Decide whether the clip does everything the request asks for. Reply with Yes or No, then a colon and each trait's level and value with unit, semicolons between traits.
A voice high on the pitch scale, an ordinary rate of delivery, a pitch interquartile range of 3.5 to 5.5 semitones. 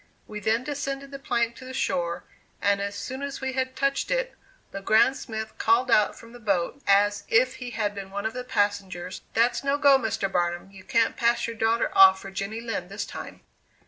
No: high, 225 Hz; fast, 210 wpm; average, 4.4 semitones